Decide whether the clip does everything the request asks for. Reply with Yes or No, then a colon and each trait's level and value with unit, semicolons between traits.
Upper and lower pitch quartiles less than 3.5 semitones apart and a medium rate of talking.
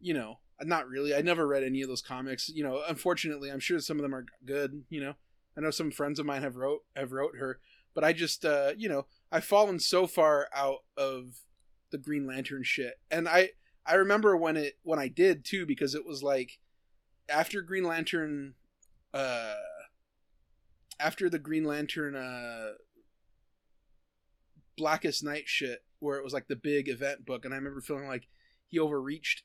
Yes: average, 3.0 semitones; average, 185 wpm